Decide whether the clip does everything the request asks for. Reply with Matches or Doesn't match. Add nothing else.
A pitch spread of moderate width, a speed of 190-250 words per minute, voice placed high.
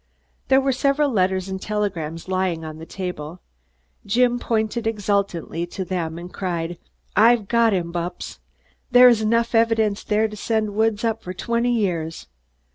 Doesn't match